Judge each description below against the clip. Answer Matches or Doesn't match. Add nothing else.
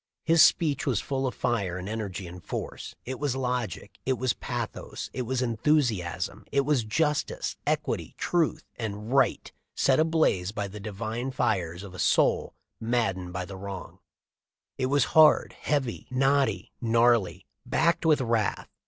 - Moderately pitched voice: Doesn't match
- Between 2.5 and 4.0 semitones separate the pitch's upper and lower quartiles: Doesn't match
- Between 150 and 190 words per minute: Matches